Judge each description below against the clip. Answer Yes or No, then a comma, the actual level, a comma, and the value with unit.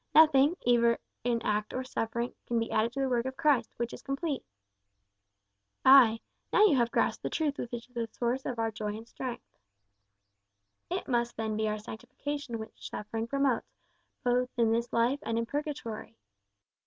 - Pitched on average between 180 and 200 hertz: No, high, 240 Hz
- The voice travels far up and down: No, average, 2.8 semitones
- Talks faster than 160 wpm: Yes, average, 175 wpm